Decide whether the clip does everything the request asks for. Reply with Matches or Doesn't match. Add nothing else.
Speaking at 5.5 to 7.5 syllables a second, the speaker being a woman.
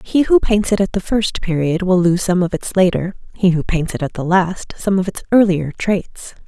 Doesn't match